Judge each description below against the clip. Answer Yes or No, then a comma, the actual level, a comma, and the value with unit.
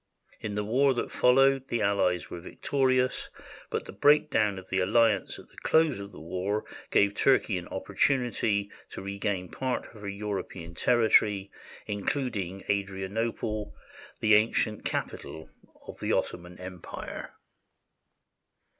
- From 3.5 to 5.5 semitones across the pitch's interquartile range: Yes, average, 3.8 semitones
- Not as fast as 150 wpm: Yes, slow, 135 wpm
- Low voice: Yes, low, 105 Hz